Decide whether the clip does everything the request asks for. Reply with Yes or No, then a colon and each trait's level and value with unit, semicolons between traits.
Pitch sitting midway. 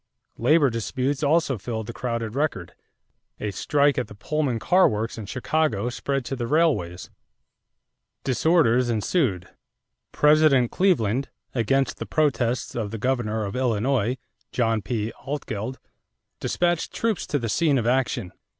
No: low, 125 Hz